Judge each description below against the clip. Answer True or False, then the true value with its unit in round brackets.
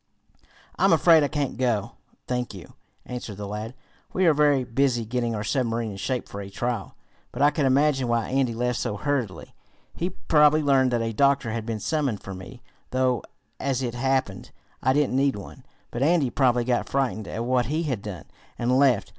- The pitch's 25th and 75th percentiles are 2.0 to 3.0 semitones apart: False (3.4 semitones)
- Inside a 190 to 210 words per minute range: True (195 wpm)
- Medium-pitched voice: False (125 Hz)